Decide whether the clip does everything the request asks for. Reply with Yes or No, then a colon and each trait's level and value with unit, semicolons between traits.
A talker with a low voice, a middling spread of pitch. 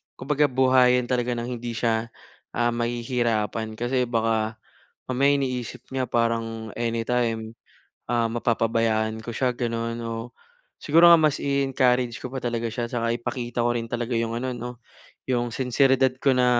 No: low, 120 Hz; narrow, 1.7 semitones